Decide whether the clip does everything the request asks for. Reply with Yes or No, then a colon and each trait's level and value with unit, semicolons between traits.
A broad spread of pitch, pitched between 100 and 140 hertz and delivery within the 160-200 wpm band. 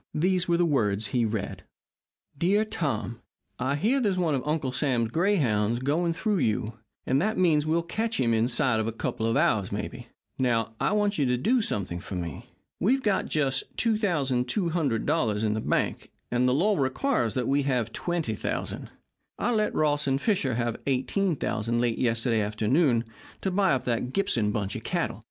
Yes: wide, 7.4 semitones; low, 135 Hz; average, 180 wpm